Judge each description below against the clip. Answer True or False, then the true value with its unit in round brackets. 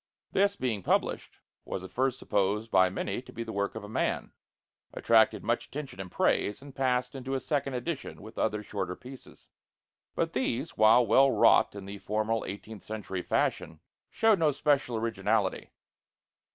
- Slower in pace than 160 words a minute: False (165 wpm)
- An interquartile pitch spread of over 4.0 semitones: True (4.7 semitones)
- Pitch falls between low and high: False (115 Hz)